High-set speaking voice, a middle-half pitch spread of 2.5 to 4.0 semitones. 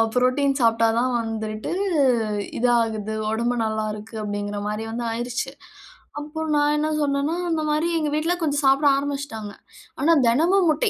No: very high, 250 Hz; average, 4.9 semitones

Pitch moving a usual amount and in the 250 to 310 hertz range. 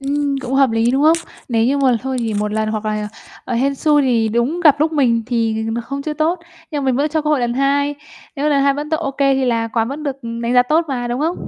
Yes: average, 3.7 semitones; very high, 270 Hz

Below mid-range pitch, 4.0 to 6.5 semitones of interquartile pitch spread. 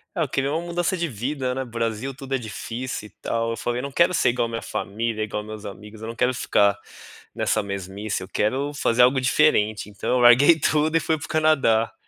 Yes: low, 120 Hz; average, 4.5 semitones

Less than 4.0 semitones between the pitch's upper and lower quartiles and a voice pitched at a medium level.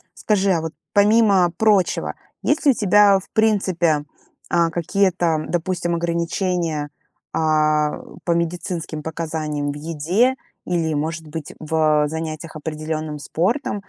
Yes: average, 3.3 semitones; medium, 165 Hz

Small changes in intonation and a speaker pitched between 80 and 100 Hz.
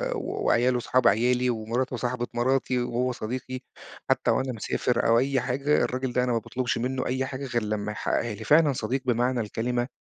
No: narrow, 1.6 semitones; low, 125 Hz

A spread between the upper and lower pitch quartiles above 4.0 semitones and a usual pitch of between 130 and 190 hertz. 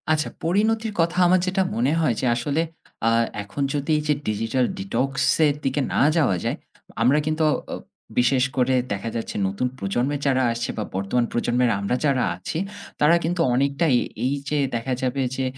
Yes: average, 4.5 semitones; low, 135 Hz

